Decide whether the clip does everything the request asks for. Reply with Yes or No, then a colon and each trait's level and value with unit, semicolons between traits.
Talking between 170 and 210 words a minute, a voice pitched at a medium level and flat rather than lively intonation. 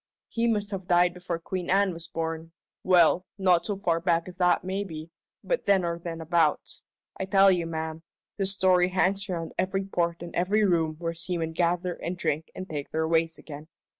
Yes: average, 190 wpm; medium, 175 Hz; narrow, 2.3 semitones